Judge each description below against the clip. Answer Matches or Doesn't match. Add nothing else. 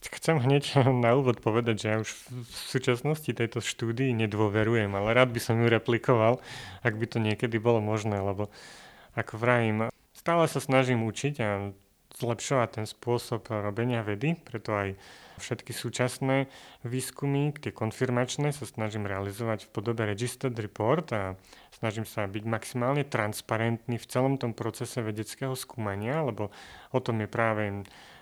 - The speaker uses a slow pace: Doesn't match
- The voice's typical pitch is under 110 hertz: Doesn't match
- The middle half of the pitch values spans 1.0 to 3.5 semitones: Matches